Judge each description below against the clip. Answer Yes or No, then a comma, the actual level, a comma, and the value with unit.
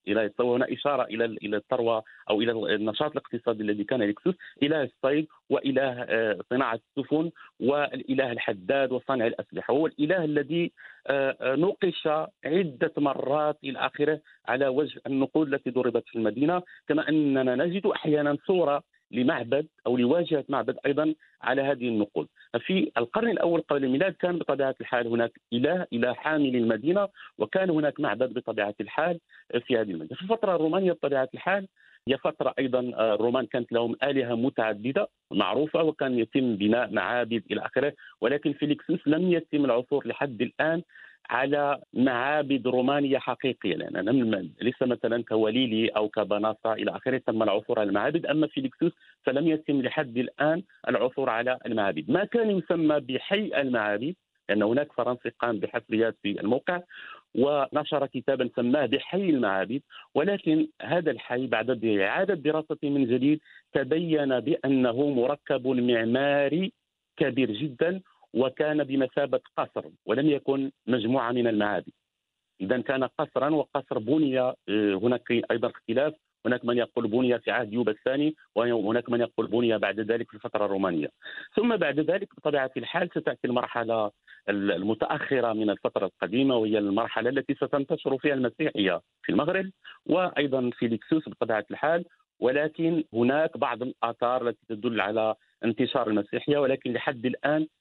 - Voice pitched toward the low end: Yes, low, 130 Hz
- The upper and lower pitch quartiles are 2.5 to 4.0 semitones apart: No, average, 4.4 semitones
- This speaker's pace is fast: Yes, fast, 140 wpm